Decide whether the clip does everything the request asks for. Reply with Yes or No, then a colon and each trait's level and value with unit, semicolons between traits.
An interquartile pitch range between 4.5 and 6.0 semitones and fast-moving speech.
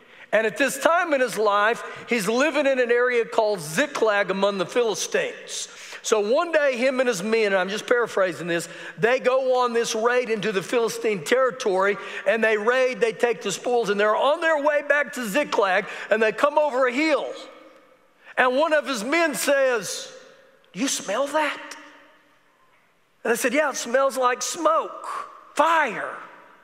No: average, 5.1 semitones; average, 175 wpm